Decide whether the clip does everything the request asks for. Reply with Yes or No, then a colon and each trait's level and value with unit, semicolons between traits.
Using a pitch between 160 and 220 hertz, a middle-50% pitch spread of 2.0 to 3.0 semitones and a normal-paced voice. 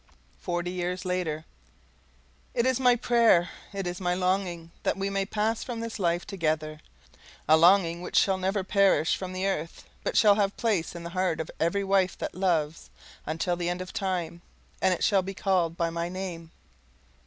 Yes: medium, 185 Hz; narrow, 2.5 semitones; average, 185 wpm